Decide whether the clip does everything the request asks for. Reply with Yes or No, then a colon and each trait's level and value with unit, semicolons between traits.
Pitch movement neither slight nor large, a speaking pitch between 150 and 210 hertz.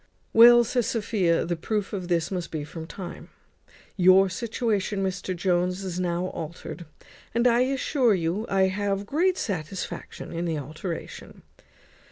Yes: average, 4.4 semitones; high, 190 Hz